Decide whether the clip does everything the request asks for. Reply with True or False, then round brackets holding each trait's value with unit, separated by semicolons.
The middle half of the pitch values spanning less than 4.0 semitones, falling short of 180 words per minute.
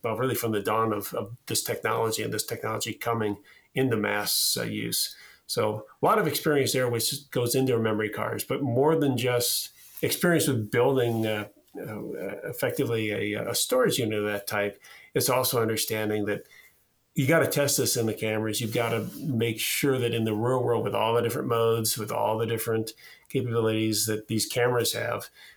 False (2.6 semitones; 185 wpm)